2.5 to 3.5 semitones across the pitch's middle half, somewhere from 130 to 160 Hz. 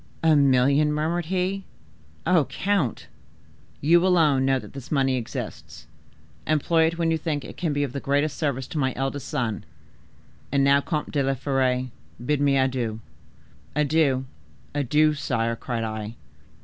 Yes: average, 2.9 semitones; medium, 140 Hz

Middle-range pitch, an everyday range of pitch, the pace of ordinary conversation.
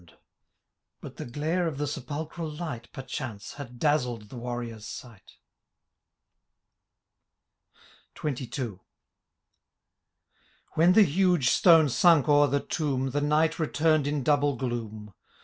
No: medium, 145 Hz; average, 4.2 semitones; slow, 115 wpm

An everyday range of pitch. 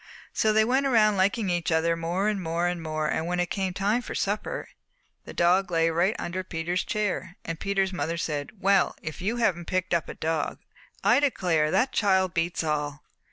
Yes: average, 3.2 semitones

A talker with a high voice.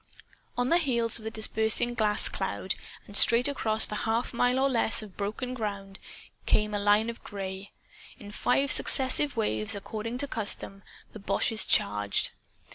Yes: high, 220 Hz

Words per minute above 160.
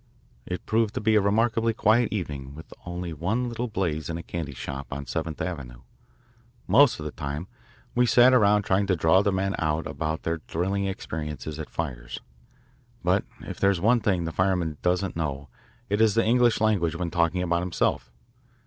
Yes: average, 185 wpm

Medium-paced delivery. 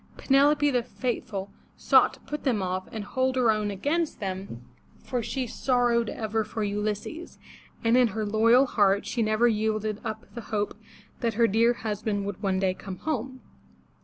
Yes: average, 170 wpm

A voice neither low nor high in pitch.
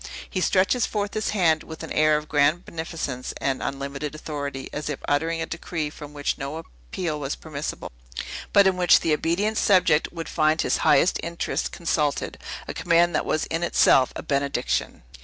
Yes: medium, 155 Hz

